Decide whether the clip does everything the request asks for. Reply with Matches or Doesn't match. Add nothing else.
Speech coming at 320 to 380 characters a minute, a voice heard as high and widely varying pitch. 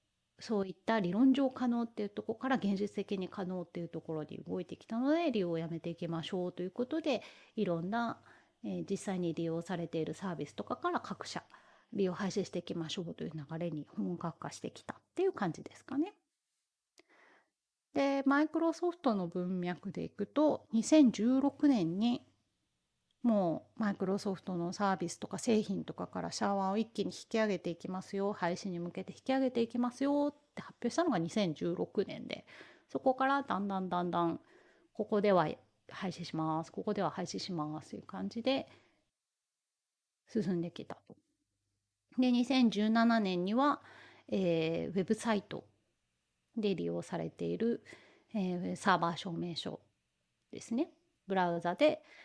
Matches